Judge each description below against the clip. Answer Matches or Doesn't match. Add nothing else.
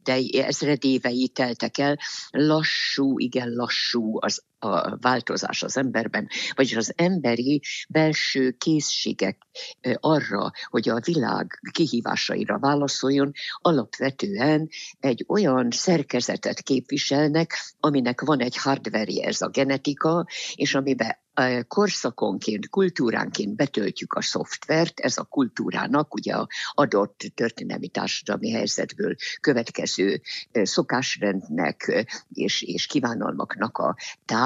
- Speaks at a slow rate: Matches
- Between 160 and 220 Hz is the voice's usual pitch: Doesn't match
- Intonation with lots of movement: Doesn't match